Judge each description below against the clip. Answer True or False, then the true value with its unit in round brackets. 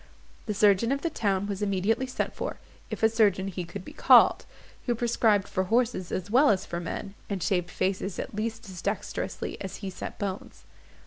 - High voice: True (200 Hz)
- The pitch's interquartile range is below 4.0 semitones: True (3.0 semitones)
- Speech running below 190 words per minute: False (195 wpm)